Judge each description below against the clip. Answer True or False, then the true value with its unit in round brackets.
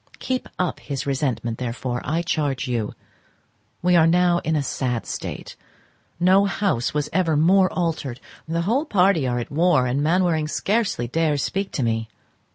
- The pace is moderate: True (165 wpm)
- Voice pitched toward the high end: False (155 Hz)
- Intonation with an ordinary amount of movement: False (5.9 semitones)